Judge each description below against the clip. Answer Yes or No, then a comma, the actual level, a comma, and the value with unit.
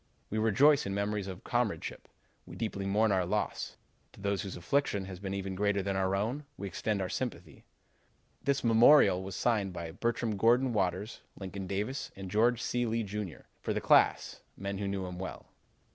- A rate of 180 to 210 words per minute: Yes, average, 190 wpm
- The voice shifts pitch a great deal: No, average, 3.1 semitones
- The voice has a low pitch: Yes, low, 100 Hz